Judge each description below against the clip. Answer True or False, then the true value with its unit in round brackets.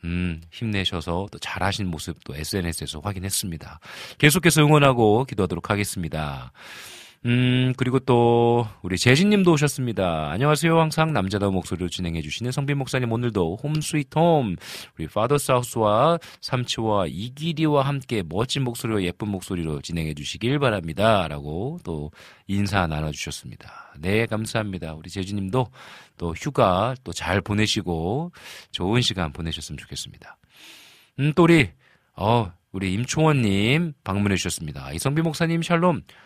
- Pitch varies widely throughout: True (7.2 semitones)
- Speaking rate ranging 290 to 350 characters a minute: True (335 characters per minute)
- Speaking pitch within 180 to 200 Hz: False (105 Hz)